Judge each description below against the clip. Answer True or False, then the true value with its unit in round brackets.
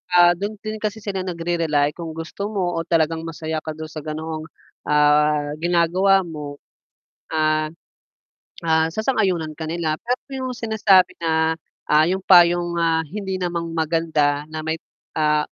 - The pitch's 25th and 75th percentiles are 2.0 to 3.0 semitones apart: True (2.6 semitones)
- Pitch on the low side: False (165 Hz)